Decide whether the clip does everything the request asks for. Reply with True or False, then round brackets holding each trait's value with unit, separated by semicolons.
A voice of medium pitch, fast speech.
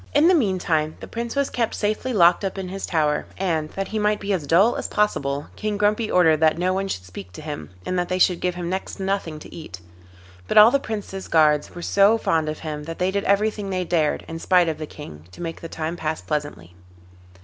True (180 Hz; 240 wpm)